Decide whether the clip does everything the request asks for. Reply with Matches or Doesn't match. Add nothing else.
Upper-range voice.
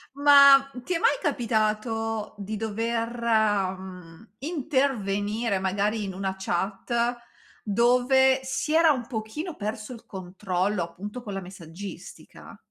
Matches